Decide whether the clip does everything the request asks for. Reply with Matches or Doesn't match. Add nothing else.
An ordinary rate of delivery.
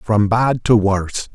Matches